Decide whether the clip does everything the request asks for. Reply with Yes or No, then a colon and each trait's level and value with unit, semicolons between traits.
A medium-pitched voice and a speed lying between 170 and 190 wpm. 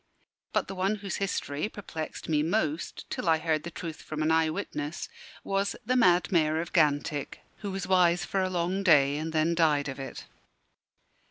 Yes: medium, 165 Hz; average, 185 wpm